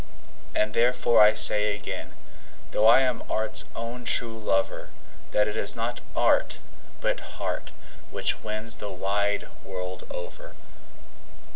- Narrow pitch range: Yes, narrow, 2.0 semitones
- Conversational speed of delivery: No, slow, 130 wpm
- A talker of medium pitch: No, low, 110 Hz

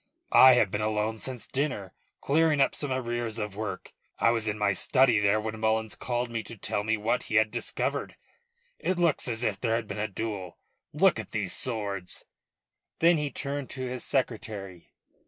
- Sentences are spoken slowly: No, average, 190 wpm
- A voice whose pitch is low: Yes, low, 110 Hz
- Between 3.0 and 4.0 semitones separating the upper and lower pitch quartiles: Yes, average, 3.4 semitones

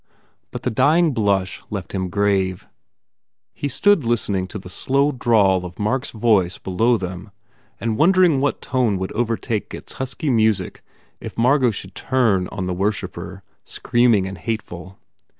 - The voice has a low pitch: Yes, low, 110 Hz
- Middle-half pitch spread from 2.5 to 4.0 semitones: No, average, 4.7 semitones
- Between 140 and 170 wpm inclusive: Yes, average, 160 wpm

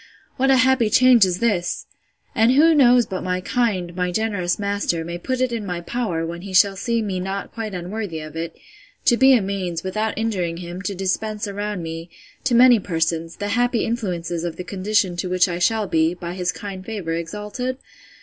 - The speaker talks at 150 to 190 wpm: No, average, 200 wpm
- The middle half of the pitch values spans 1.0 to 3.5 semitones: No, average, 4.3 semitones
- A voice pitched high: Yes, high, 195 Hz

